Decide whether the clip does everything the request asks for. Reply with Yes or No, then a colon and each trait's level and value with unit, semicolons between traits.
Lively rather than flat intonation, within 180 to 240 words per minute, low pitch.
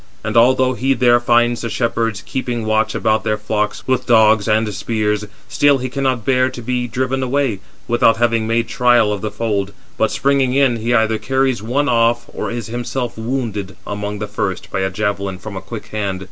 No: average, 2.8 semitones; average, 195 wpm; low, 115 Hz